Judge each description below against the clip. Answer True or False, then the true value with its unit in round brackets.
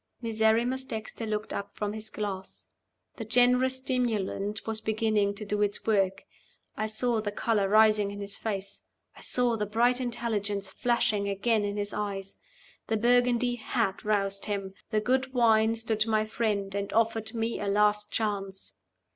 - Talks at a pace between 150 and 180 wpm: True (160 wpm)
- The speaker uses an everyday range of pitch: False (2.2 semitones)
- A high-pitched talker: True (215 Hz)